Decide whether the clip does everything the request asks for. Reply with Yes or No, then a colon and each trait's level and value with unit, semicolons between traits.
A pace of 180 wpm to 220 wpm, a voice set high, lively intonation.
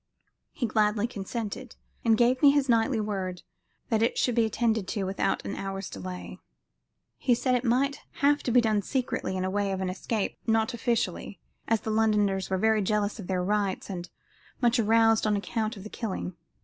No: average, 190 wpm; high, 220 Hz; average, 3.1 semitones